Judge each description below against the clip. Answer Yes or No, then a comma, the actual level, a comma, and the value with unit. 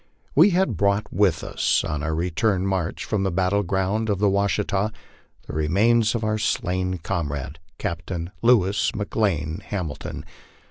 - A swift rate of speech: No, average, 150 wpm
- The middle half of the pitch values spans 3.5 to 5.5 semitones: Yes, average, 3.8 semitones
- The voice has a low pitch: Yes, very low, 95 Hz